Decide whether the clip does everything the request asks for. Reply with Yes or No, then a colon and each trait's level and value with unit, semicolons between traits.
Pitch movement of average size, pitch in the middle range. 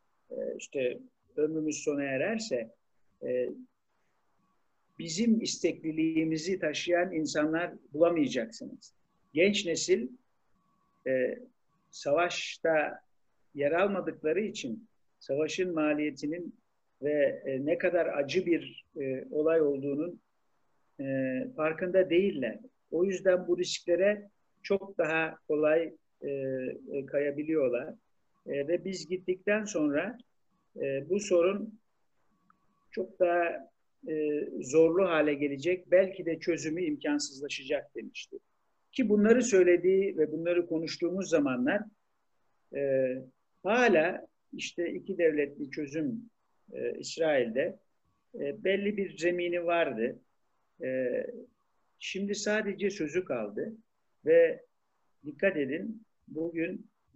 Yes: average, 5.0 semitones; medium, 175 Hz